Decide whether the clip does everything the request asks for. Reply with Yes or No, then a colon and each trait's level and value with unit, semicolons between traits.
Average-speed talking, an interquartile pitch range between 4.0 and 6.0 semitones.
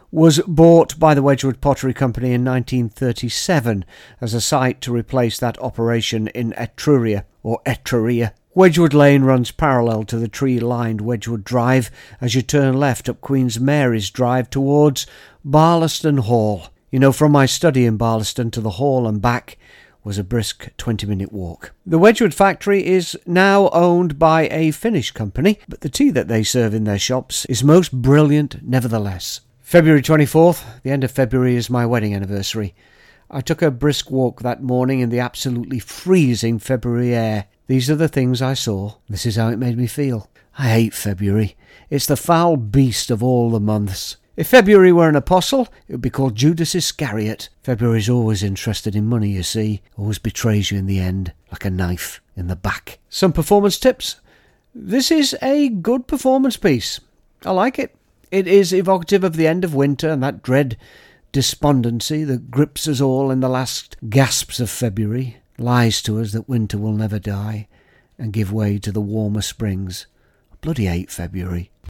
Yes: average, 180 wpm; average, 5.2 semitones